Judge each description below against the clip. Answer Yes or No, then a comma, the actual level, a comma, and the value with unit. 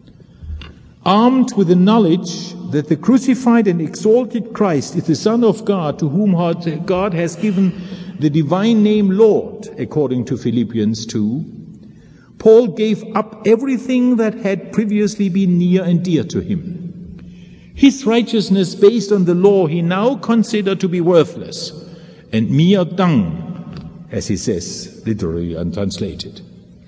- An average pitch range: Yes, average, 4.6 semitones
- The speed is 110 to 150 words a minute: Yes, average, 140 wpm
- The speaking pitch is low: No, medium, 185 Hz